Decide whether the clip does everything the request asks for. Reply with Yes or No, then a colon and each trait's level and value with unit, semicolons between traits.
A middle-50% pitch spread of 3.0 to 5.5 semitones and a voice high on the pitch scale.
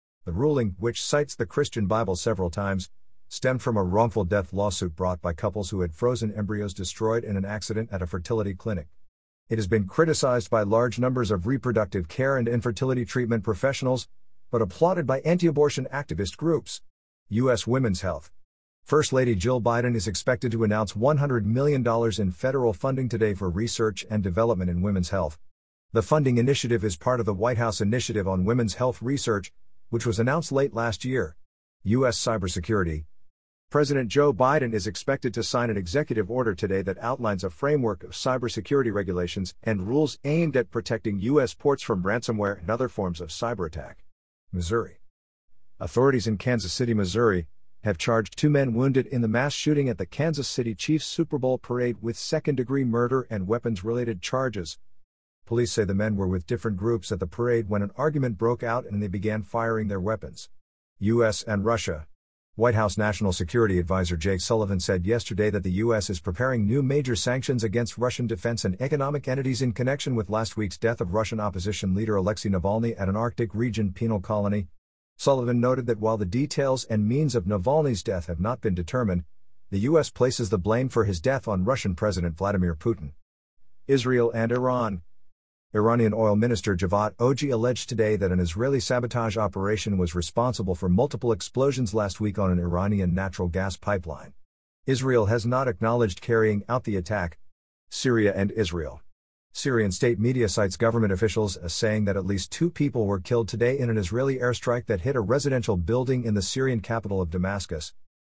No: average, 4.3 semitones; low, 110 Hz